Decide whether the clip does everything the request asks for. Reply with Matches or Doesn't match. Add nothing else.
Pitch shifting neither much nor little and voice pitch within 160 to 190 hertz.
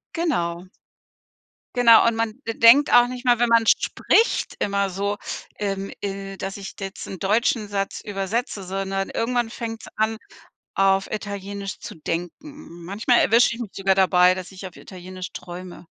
Doesn't match